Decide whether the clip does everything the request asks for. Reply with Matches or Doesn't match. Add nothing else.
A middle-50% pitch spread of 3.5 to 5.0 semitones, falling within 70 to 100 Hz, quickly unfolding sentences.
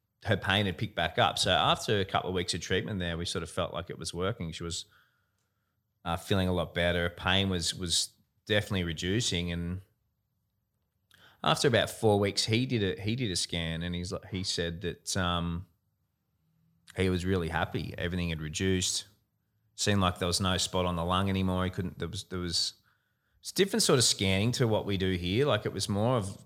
Doesn't match